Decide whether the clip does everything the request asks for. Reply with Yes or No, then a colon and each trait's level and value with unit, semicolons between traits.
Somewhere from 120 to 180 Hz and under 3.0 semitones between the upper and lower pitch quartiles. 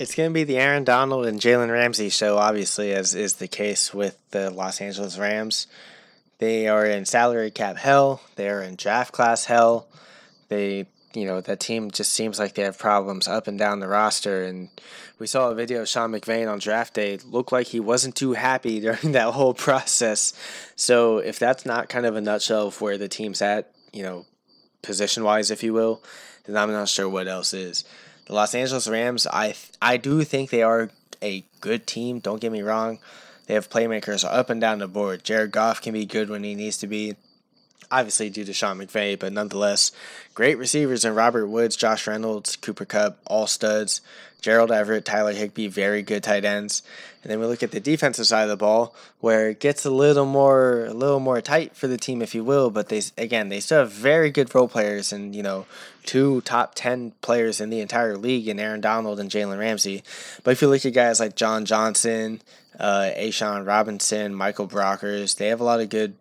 No: low, 110 Hz; narrow, 2.6 semitones